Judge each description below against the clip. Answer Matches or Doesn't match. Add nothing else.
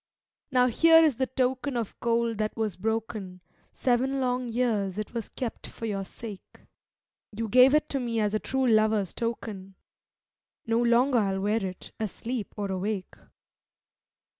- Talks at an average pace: Matches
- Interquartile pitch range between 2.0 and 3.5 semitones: Matches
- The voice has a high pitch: Matches